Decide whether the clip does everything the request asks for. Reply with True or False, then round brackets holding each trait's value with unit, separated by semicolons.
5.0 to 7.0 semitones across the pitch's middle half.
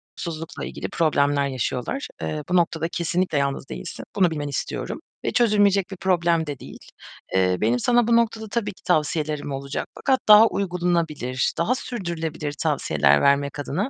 True (5.4 semitones)